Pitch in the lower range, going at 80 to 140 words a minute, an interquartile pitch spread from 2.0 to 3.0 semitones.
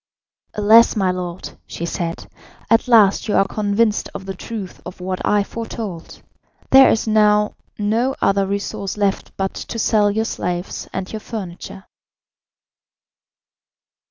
No: high, 205 Hz; slow, 135 wpm; narrow, 2.5 semitones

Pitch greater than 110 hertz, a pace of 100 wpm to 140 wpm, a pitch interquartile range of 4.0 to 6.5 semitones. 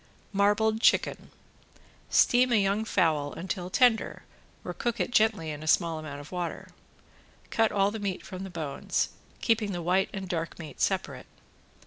No: high, 190 Hz; average, 160 wpm; average, 4.8 semitones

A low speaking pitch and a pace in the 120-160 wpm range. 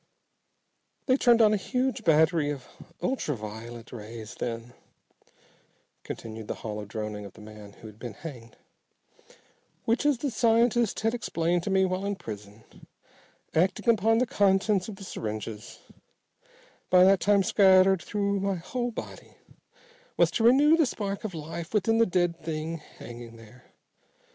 No: medium, 180 Hz; average, 150 wpm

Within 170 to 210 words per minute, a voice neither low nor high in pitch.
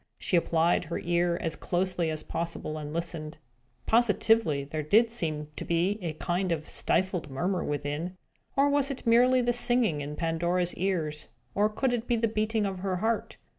Yes: average, 175 wpm; medium, 180 Hz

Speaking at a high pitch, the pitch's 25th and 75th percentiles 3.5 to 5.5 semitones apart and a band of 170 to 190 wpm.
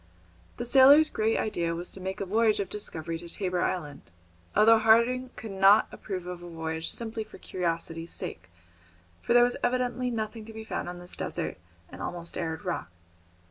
Yes: high, 200 Hz; average, 4.6 semitones; average, 180 wpm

